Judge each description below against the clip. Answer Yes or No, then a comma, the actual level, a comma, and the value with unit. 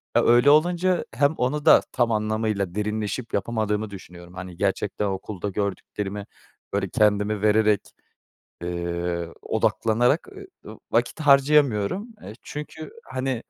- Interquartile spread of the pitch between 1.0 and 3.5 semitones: No, average, 4.6 semitones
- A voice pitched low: Yes, low, 105 Hz